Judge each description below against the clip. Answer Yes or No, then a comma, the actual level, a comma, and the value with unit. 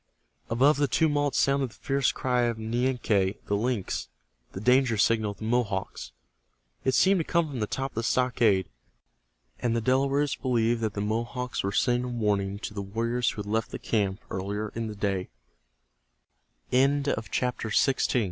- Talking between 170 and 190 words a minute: No, average, 155 wpm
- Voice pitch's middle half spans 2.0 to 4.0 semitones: Yes, average, 3.7 semitones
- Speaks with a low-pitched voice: Yes, low, 115 Hz